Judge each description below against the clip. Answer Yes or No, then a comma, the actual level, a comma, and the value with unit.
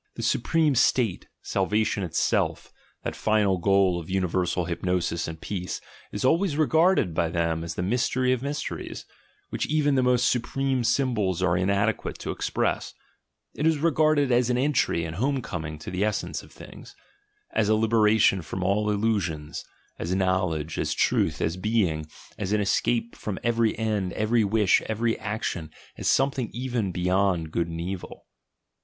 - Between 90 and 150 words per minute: No, average, 160 wpm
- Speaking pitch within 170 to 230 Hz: No, low, 105 Hz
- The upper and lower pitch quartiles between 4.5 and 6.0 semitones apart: Yes, average, 5.3 semitones